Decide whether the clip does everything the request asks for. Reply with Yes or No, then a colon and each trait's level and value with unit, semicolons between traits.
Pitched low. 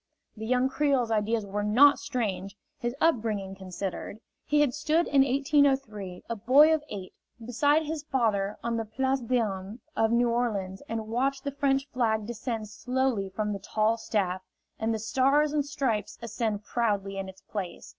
No: high, 230 Hz